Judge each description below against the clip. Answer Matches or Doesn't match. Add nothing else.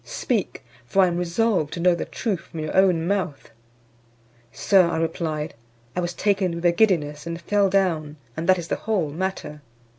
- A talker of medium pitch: Matches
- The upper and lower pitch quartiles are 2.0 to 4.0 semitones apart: Matches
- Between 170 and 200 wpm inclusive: Matches